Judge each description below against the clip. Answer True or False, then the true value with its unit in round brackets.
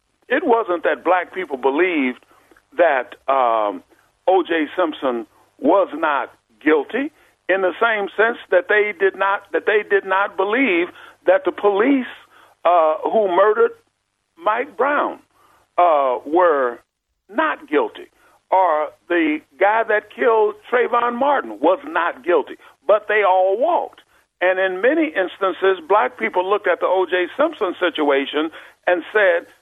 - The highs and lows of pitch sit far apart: True (7.5 semitones)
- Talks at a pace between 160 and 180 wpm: False (135 wpm)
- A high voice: True (210 Hz)